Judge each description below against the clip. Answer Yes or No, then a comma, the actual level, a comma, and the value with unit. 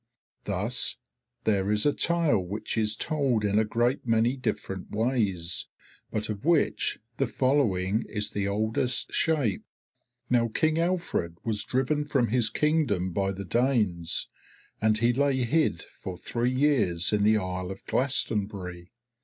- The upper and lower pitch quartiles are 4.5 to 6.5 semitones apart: Yes, average, 4.9 semitones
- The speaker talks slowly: No, average, 145 wpm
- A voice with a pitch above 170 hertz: No, low, 110 Hz